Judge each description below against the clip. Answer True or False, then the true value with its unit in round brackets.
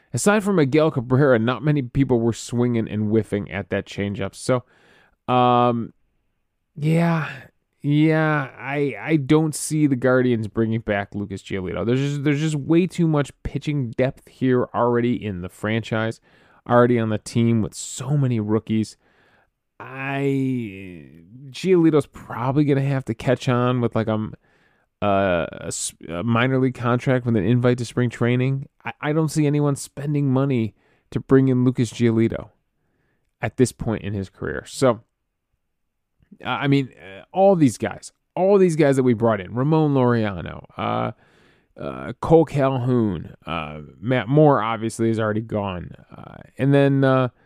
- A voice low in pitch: True (125 Hz)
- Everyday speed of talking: True (150 wpm)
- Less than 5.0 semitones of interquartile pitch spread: True (4.4 semitones)